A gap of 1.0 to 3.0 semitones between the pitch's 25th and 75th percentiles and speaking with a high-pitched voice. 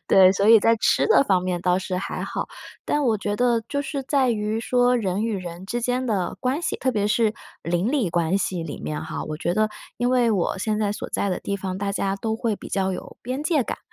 No: average, 4.6 semitones; high, 210 Hz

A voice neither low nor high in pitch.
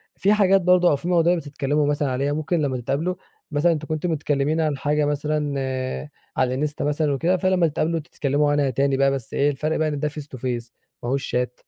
Yes: medium, 150 Hz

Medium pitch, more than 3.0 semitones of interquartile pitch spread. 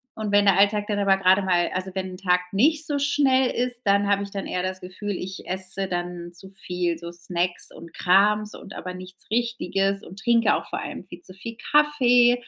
No: high, 195 Hz; average, 3.4 semitones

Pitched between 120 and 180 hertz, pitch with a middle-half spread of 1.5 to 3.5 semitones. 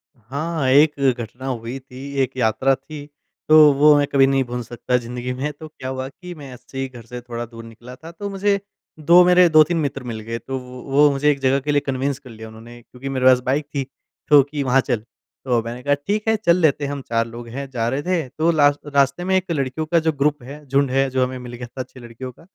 Yes: low, 135 Hz; average, 3.2 semitones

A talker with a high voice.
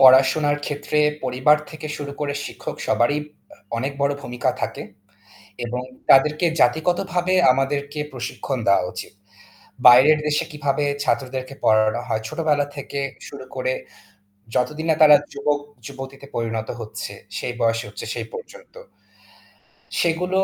No: medium, 140 Hz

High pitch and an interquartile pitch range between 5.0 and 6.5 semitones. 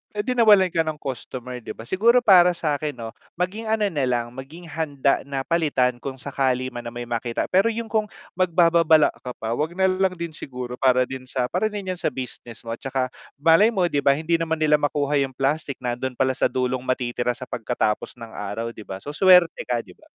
No: medium, 140 Hz; wide, 5.6 semitones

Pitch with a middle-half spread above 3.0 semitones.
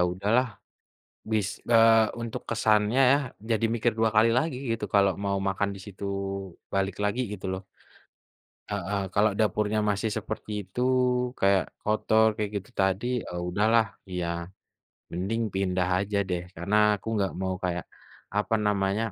No: narrow, 2.4 semitones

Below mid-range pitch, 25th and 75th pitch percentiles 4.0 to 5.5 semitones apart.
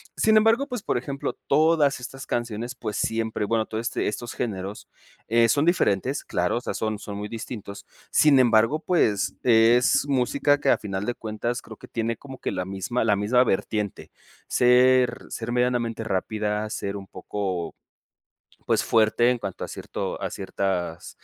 No: low, 115 Hz; average, 3.3 semitones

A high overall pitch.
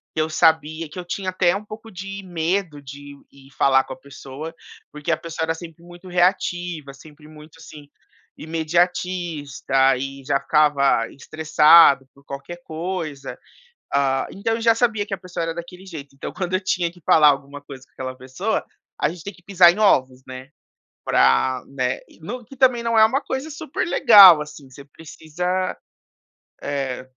No: medium, 160 Hz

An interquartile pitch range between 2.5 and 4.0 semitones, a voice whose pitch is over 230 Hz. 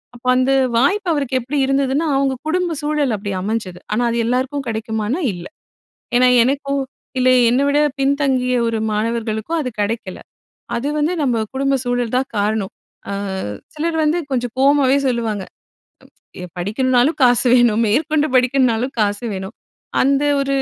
Yes: average, 3.7 semitones; very high, 255 Hz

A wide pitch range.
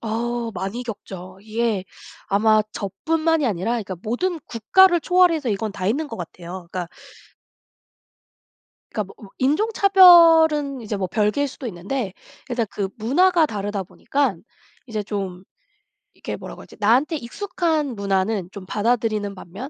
Yes: wide, 6.8 semitones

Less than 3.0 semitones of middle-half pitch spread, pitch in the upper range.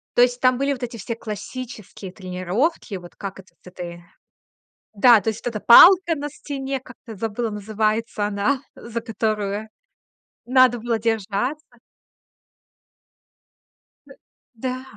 No: average, 3.7 semitones; high, 225 Hz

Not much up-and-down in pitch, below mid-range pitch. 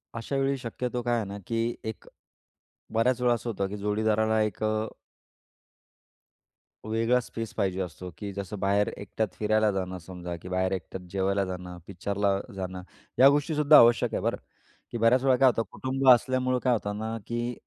No: average, 3.7 semitones; low, 110 Hz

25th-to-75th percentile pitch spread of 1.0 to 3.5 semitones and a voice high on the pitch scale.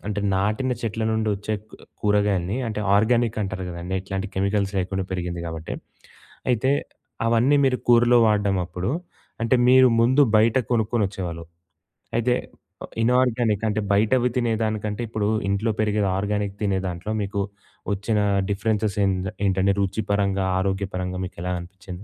No: average, 2.8 semitones; low, 105 Hz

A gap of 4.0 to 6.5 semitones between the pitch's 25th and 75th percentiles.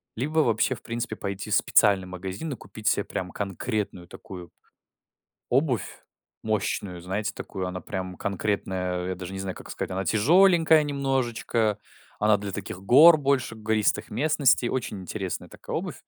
Yes: average, 4.8 semitones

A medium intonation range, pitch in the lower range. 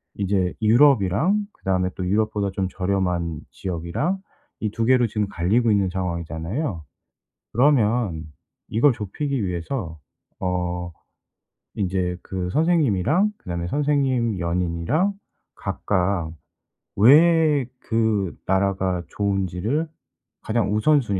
No: wide, 5.7 semitones; low, 100 Hz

